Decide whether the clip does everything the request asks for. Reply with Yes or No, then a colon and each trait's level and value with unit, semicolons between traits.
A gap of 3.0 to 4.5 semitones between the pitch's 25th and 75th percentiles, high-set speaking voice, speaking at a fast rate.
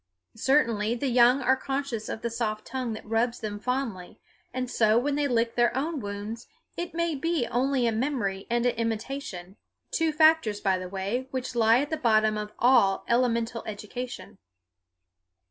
No: average, 3.5 semitones; high, 235 Hz; average, 170 wpm